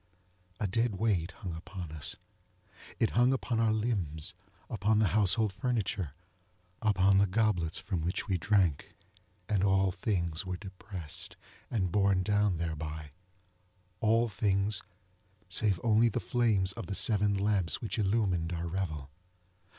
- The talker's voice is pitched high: No, very low, 95 Hz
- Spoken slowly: Yes, slow, 125 wpm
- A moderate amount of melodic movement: Yes, average, 3.1 semitones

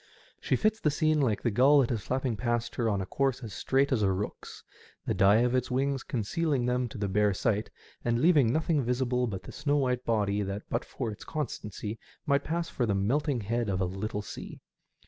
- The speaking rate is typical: No, fast, 220 wpm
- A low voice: Yes, low, 120 Hz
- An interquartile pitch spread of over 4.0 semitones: Yes, average, 4.6 semitones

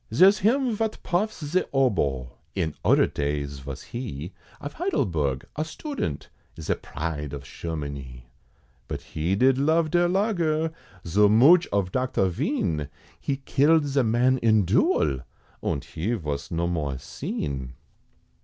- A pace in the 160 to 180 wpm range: No, slow, 135 wpm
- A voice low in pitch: Yes, low, 100 Hz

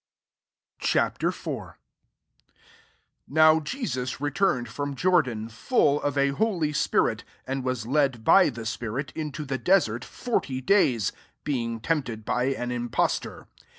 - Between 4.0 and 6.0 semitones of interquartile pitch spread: Yes, average, 4.3 semitones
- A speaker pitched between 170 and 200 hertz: No, low, 135 Hz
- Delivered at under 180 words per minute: Yes, average, 145 wpm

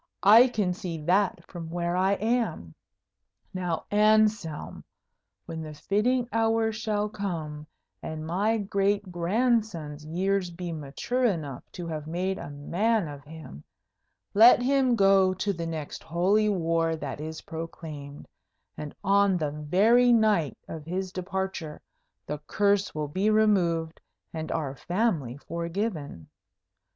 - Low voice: No, medium, 180 Hz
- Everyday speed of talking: No, slow, 130 wpm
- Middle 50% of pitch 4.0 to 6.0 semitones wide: Yes, average, 4.7 semitones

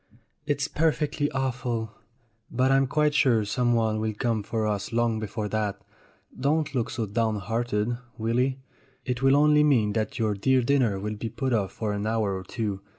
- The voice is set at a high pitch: No, low, 115 Hz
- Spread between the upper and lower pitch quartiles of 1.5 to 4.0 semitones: Yes, average, 3.7 semitones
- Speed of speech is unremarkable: Yes, average, 170 wpm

